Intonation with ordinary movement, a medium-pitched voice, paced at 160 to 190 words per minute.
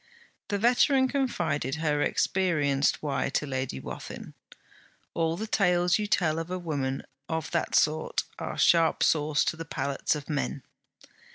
No: average, 3.5 semitones; medium, 160 Hz; average, 150 wpm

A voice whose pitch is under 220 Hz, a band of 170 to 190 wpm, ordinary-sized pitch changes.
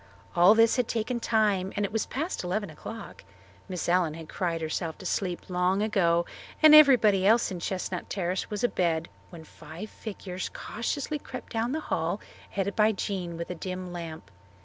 Yes: high, 190 Hz; average, 175 wpm; average, 4.2 semitones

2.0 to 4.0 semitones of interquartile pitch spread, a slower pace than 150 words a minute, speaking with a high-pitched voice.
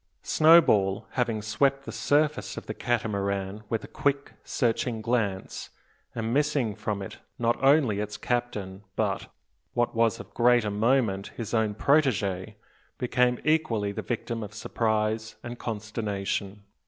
No: average, 3.0 semitones; slow, 135 wpm; low, 115 Hz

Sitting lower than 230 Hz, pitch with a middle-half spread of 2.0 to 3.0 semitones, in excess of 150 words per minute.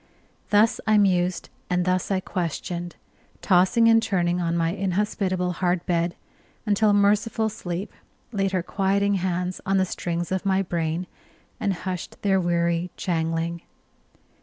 No: medium, 185 Hz; narrow, 2.4 semitones; slow, 135 wpm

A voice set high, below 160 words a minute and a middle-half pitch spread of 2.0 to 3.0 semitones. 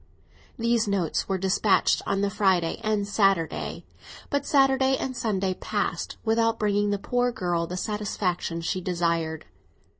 No: high, 200 Hz; average, 140 wpm; average, 3.9 semitones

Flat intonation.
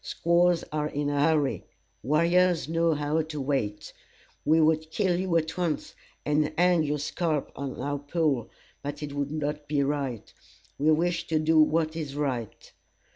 Yes: narrow, 2.3 semitones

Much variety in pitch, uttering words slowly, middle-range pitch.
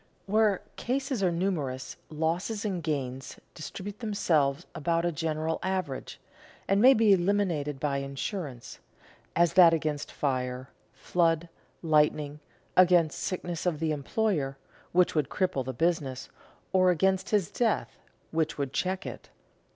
No: average, 4.6 semitones; slow, 130 wpm; medium, 165 Hz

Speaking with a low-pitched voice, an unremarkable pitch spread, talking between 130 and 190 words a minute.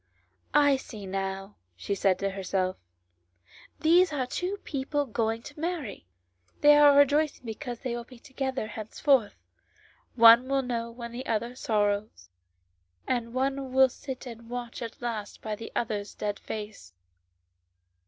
No: high, 235 Hz; average, 4.2 semitones; average, 145 wpm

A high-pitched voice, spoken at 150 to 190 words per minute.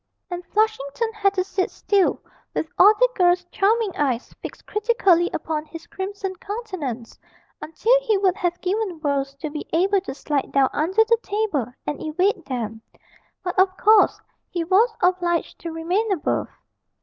Yes: very high, 365 Hz; average, 160 wpm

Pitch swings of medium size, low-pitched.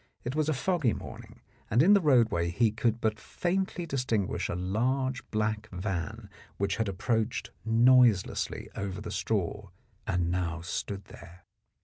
Yes: average, 5.0 semitones; low, 110 Hz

